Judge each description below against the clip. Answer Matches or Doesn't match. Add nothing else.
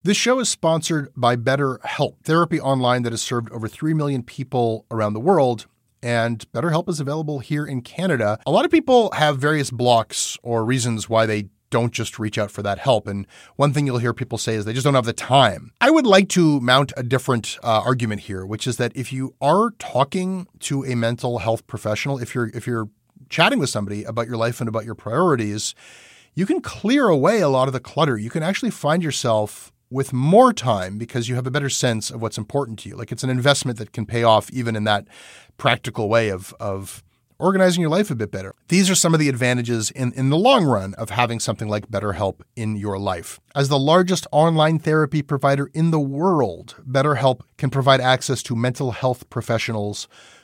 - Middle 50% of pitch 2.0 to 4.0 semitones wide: Doesn't match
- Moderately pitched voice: Doesn't match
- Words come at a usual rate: Doesn't match